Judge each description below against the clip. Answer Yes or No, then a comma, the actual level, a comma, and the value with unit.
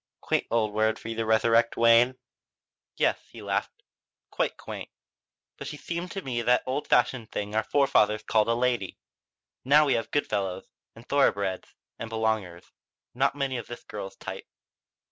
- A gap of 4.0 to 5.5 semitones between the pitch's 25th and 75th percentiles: No, average, 3.1 semitones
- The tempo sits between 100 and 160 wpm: No, average, 170 wpm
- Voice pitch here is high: No, low, 115 Hz